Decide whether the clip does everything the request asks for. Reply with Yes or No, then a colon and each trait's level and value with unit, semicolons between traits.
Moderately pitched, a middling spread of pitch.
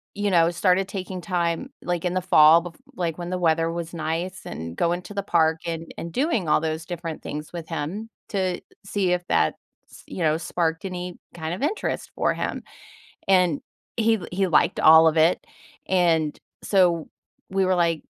No: medium, 175 Hz; narrow, 2.3 semitones